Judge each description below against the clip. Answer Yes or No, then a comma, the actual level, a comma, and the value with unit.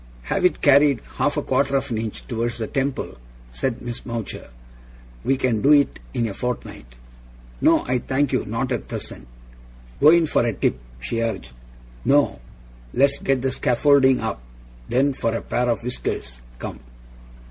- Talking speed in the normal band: Yes, average, 170 wpm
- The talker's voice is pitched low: Yes, low, 125 Hz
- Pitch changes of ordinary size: Yes, average, 3.3 semitones